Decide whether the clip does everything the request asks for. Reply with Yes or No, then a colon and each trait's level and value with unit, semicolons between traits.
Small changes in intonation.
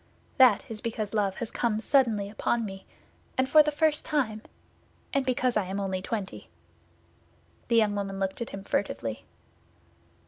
No: average, 4.3 semitones